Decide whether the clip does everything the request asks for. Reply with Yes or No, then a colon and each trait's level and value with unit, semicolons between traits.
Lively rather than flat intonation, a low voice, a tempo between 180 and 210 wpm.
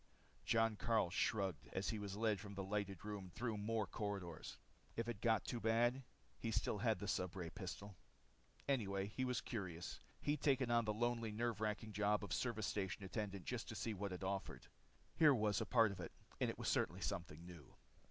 No: average, 2.8 semitones; low, 105 Hz; average, 195 wpm